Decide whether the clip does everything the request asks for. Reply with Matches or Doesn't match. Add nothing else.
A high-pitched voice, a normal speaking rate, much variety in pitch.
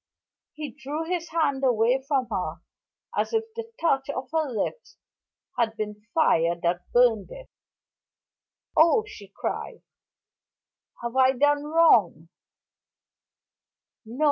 Doesn't match